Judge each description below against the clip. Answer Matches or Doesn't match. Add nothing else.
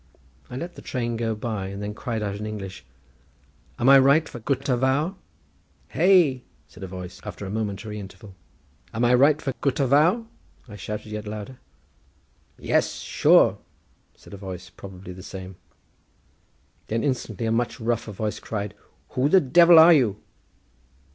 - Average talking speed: Matches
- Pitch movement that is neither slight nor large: Matches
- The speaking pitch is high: Doesn't match